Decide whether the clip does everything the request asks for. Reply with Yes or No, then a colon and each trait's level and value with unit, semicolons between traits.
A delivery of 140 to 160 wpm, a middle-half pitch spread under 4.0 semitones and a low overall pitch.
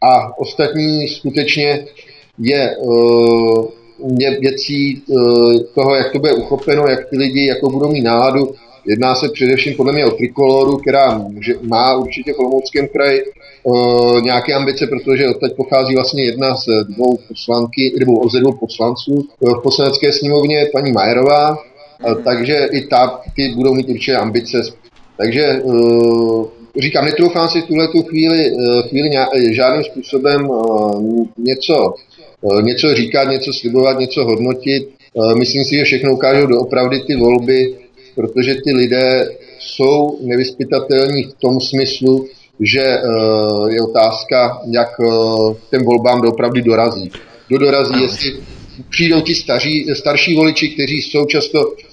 No: average, 125 wpm; average, 2.7 semitones; low, 130 Hz